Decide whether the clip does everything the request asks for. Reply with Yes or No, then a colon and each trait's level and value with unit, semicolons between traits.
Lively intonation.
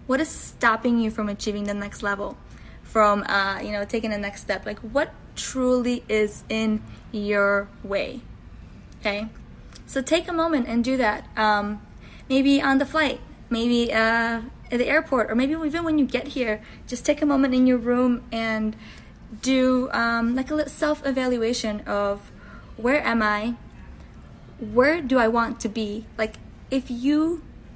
No: average, 3.8 semitones